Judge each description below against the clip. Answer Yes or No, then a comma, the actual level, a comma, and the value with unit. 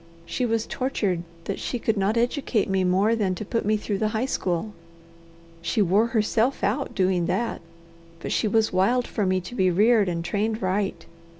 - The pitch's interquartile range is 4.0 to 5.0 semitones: No, average, 3.4 semitones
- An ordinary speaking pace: Yes, average, 190 wpm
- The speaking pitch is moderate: No, high, 210 Hz